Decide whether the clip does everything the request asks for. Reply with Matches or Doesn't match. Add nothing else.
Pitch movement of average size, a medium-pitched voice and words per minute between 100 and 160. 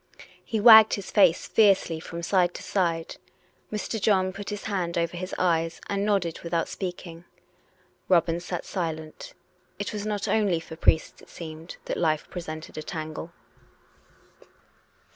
Matches